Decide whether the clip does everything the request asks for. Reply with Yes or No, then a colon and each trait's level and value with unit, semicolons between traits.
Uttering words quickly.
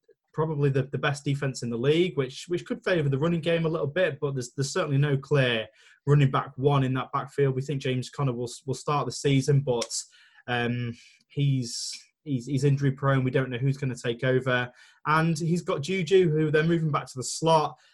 Yes: fast, 215 wpm